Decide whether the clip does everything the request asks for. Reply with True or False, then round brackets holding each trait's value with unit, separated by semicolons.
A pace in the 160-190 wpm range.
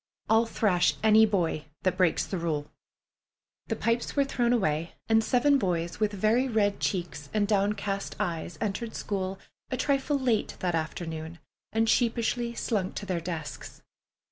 False (150 wpm)